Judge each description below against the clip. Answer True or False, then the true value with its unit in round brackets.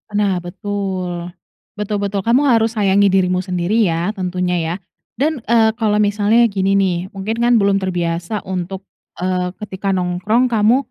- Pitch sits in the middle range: False (195 Hz)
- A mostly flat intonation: False (3.0 semitones)